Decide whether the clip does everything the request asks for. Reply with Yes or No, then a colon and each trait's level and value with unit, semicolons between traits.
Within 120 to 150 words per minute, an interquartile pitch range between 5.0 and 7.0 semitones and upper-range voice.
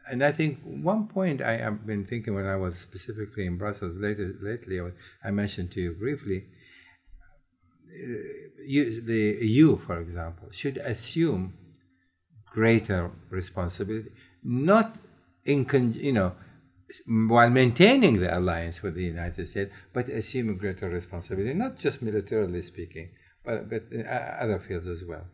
No: slow, 135 wpm; wide, 5.4 semitones; low, 105 Hz